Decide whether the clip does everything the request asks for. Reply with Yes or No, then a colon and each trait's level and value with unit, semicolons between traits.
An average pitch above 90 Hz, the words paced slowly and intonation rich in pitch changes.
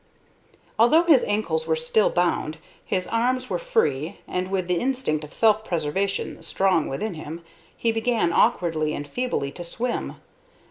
No: medium, 185 Hz; average, 150 wpm; wide, 6.1 semitones